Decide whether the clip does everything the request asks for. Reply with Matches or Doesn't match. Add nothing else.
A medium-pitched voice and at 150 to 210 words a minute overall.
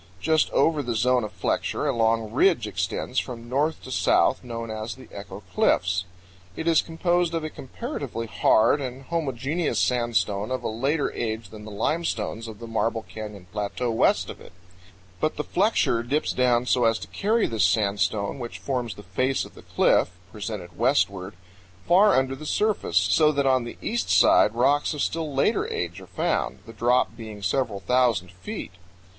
Doesn't match